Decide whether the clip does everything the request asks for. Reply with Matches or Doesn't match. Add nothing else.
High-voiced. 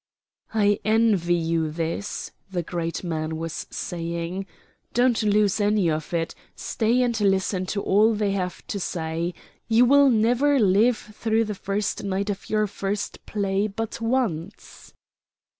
Matches